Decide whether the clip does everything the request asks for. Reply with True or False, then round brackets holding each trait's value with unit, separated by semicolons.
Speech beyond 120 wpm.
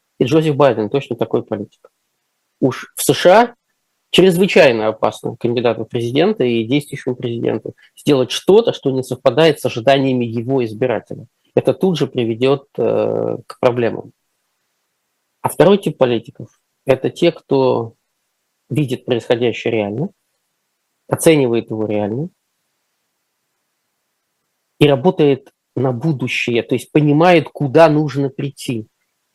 False (110 wpm)